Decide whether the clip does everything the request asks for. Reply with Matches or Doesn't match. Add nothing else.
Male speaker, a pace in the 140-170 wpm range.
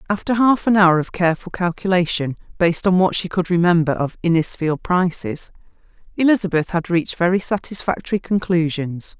Doesn't match